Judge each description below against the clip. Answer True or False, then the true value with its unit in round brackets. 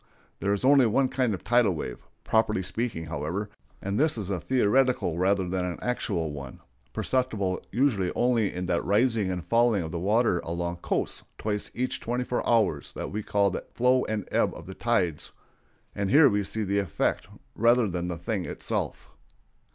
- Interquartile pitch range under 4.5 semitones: False (5.1 semitones)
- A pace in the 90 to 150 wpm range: False (180 wpm)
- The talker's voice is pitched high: False (100 Hz)